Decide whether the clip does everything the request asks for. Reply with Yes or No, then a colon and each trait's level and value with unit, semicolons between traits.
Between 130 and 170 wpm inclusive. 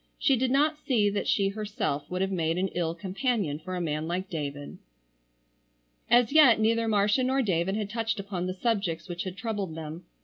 No: average, 195 wpm